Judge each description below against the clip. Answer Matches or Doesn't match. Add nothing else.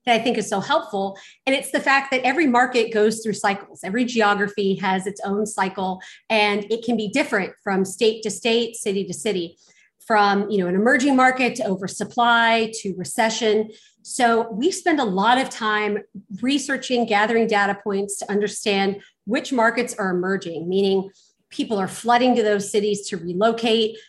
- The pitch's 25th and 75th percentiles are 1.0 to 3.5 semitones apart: Matches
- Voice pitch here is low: Doesn't match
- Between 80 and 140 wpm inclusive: Doesn't match